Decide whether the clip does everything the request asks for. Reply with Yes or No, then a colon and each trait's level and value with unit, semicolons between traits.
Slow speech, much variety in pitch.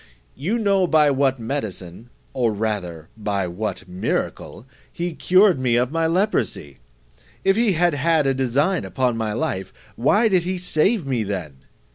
No: average, 155 wpm; wide, 8.5 semitones